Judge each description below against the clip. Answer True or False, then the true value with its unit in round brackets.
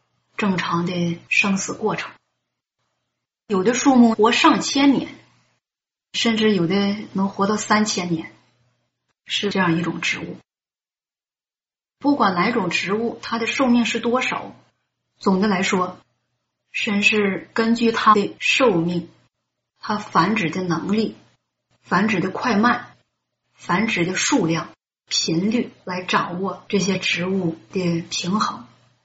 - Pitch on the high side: True (195 Hz)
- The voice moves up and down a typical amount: True (4.4 semitones)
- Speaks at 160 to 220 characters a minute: True (175 characters per minute)